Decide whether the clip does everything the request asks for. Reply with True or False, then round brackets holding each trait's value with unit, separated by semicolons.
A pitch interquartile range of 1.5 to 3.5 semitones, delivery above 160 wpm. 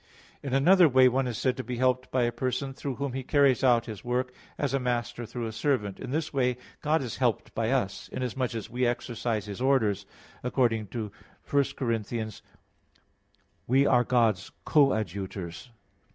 True (2.9 semitones; 180 wpm)